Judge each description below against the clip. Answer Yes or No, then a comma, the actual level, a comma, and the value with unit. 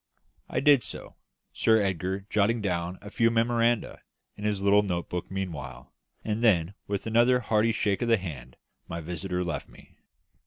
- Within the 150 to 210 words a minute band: Yes, average, 160 wpm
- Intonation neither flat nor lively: Yes, average, 4.3 semitones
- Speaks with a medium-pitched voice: No, low, 100 Hz